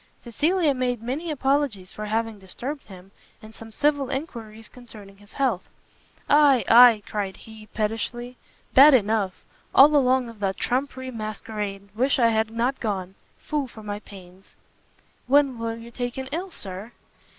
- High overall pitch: Yes, high, 230 Hz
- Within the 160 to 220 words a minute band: No, average, 150 wpm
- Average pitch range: Yes, average, 4.0 semitones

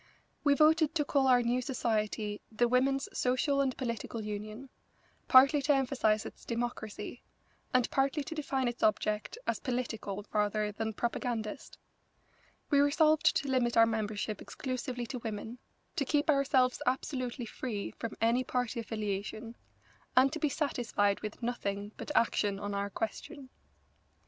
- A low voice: No, high, 245 Hz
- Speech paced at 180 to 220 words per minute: No, average, 145 wpm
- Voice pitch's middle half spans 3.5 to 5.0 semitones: Yes, average, 4.0 semitones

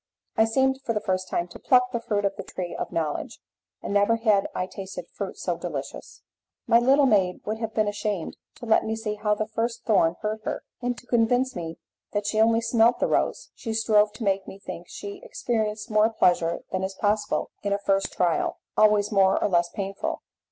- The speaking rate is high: Yes, fast, 210 wpm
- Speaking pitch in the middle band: No, high, 210 Hz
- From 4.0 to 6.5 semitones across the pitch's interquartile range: No, narrow, 2.6 semitones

